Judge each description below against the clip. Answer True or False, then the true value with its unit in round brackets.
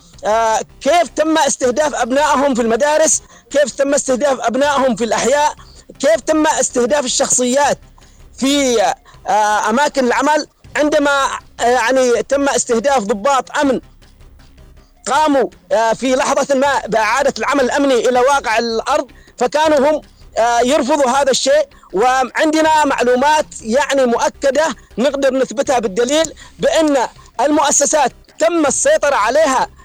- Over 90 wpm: True (115 wpm)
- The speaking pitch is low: False (275 Hz)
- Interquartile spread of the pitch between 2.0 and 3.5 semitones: True (3.2 semitones)